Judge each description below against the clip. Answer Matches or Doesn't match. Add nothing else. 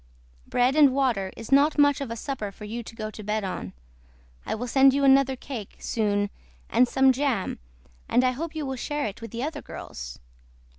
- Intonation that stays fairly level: Doesn't match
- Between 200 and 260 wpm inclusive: Matches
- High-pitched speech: Matches